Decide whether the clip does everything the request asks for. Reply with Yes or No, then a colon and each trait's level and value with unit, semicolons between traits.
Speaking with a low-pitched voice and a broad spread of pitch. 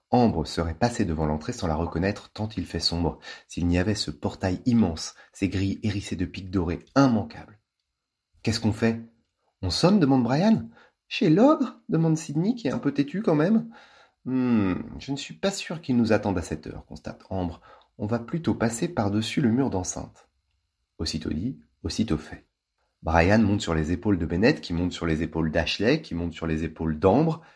Yes: low, 100 Hz; wide, 6.8 semitones